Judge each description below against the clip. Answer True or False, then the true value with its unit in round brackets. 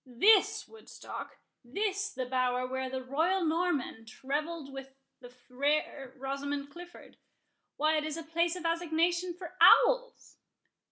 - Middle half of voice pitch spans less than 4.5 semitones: False (4.8 semitones)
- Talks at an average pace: False (120 wpm)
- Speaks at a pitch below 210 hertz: False (305 Hz)